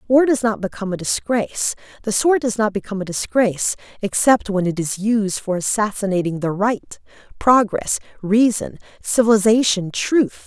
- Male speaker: No, female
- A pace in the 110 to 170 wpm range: Yes, average, 150 wpm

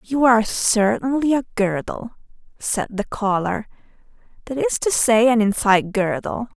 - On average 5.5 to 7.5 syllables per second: No, 4.6 syllables/s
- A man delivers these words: No, female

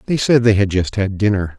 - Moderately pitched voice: No, low, 105 Hz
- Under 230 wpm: No, fast, 265 wpm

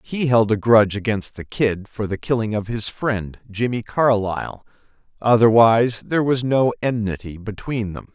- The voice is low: Yes, low, 110 Hz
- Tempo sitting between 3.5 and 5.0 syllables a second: Yes, 4.9 syllables/s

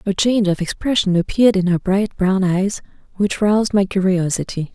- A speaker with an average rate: Yes, average, 175 wpm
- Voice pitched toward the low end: No, high, 195 Hz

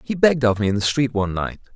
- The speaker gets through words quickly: Yes, fast, 310 wpm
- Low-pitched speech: Yes, low, 115 Hz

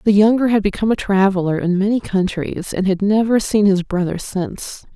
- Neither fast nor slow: Yes, average, 195 wpm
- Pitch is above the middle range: Yes, high, 200 Hz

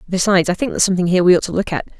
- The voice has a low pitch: No, medium, 180 Hz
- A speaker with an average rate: No, fast, 330 wpm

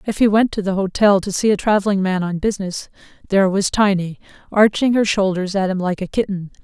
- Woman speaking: Yes, female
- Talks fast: Yes, fast, 215 wpm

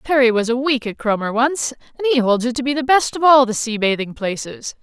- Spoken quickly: Yes, fast, 260 wpm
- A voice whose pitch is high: Yes, very high, 250 Hz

